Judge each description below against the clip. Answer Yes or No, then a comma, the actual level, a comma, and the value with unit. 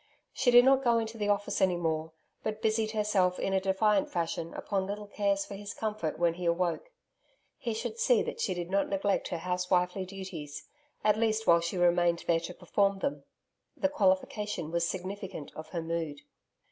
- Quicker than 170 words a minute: Yes, average, 190 wpm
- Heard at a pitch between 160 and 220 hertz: Yes, high, 190 Hz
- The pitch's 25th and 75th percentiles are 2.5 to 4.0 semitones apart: Yes, average, 3.5 semitones